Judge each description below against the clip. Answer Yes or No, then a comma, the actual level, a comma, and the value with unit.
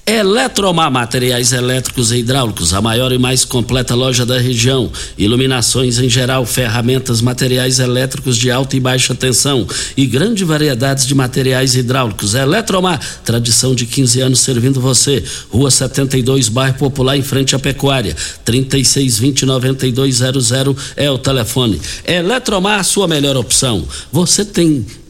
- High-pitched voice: No, low, 130 Hz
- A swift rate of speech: No, average, 135 wpm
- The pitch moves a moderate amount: No, narrow, 1.5 semitones